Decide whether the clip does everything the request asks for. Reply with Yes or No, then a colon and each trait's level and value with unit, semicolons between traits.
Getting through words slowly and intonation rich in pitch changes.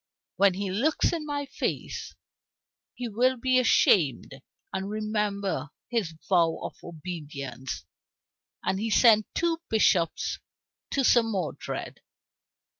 Yes: slow, 115 wpm; wide, 6.2 semitones